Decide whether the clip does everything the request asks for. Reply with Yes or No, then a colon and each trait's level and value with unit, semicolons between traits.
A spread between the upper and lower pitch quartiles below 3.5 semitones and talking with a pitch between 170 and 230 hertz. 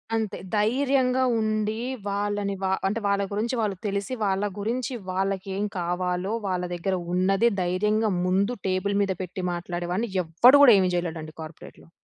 Yes: average, 2.9 semitones; high, 200 Hz